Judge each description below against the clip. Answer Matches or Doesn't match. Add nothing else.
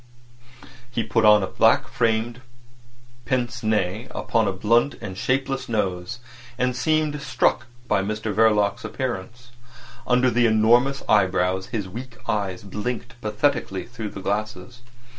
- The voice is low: Matches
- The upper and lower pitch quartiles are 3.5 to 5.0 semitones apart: Doesn't match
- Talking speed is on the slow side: Matches